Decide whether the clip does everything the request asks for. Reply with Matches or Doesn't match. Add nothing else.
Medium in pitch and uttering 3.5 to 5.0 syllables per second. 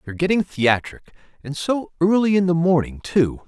Doesn't match